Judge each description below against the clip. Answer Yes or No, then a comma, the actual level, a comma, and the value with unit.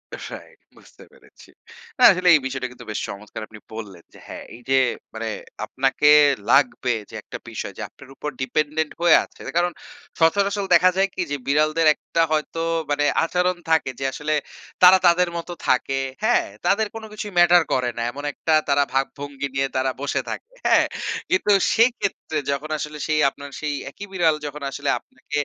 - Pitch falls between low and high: Yes, medium, 150 Hz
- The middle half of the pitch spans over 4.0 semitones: Yes, average, 4.7 semitones